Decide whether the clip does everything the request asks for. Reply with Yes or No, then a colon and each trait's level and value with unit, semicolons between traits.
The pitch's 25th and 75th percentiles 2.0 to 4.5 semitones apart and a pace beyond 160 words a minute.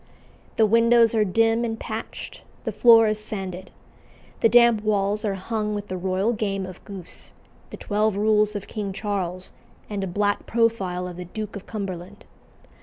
Yes: narrow, 2.5 semitones; average, 170 wpm